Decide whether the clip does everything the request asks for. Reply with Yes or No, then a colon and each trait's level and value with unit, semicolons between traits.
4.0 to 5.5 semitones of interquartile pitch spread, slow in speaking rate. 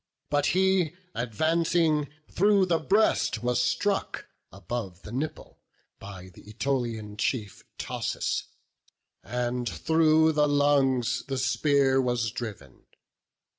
Yes: average, 5.1 semitones; slow, 105 wpm